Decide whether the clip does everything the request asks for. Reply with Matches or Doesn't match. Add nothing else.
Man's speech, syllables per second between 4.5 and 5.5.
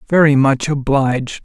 Matches